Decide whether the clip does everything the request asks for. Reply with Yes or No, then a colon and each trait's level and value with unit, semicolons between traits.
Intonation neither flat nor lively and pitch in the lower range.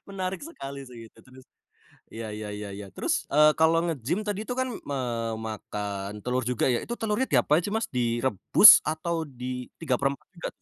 No: wide, 6.5 semitones; low, 130 Hz